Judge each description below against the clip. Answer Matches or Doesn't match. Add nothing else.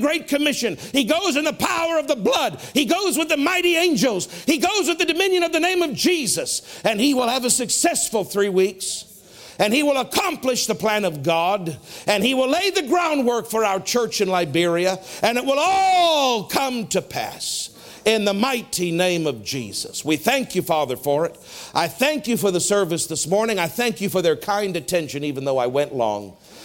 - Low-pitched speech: Doesn't match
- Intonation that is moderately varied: Doesn't match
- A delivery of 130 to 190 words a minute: Doesn't match